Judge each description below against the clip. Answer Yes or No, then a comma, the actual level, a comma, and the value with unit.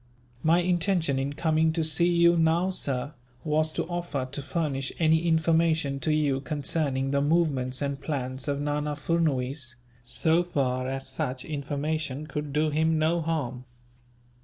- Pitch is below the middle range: No, medium, 150 Hz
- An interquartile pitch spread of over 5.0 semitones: No, average, 2.9 semitones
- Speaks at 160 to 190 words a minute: No, average, 150 wpm